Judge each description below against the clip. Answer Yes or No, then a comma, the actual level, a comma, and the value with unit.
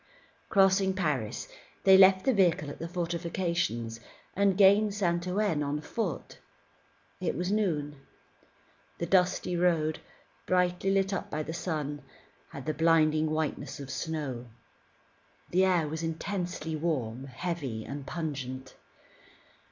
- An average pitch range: Yes, average, 4.1 semitones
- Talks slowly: Yes, slow, 125 wpm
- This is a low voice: No, medium, 165 Hz